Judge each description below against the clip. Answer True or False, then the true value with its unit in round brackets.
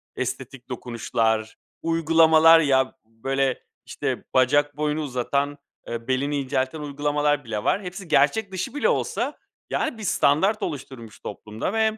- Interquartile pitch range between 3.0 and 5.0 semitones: True (4.1 semitones)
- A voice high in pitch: False (145 Hz)